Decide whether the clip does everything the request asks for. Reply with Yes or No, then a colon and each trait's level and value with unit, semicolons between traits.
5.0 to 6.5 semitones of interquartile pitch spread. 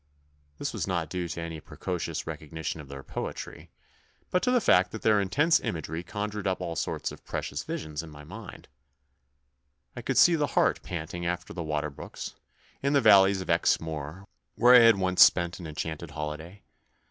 No: average, 3.8 semitones